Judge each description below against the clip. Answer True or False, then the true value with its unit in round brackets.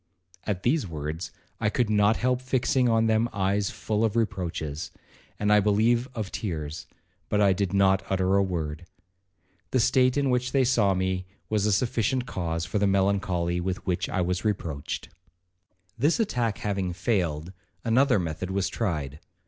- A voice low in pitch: True (100 Hz)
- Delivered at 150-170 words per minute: True (160 wpm)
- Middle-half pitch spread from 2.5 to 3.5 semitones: False (4.0 semitones)